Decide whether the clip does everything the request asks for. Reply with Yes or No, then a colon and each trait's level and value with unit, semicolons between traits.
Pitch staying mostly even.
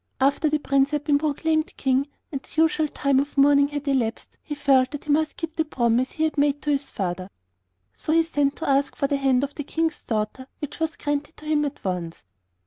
Yes: narrow, 2.2 semitones